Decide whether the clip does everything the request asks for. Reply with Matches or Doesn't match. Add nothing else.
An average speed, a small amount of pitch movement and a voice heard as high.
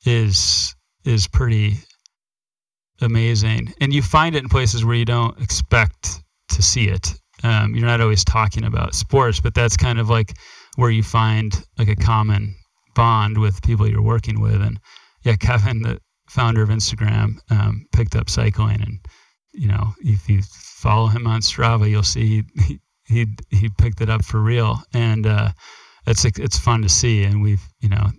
Doesn't match